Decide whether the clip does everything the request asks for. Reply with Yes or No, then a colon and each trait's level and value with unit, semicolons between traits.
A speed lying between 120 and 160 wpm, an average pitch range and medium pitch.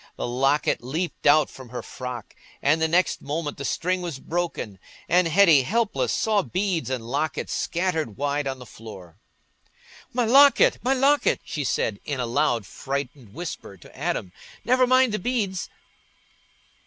No: average, 155 wpm; wide, 6.4 semitones; medium, 155 Hz